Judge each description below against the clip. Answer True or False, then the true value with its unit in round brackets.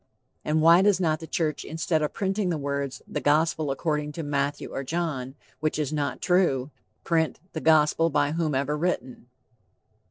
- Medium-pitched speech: True (155 Hz)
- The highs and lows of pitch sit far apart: False (2.4 semitones)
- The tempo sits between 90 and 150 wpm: False (165 wpm)